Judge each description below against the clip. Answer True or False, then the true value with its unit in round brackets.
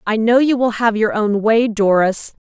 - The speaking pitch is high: True (220 Hz)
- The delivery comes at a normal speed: False (220 wpm)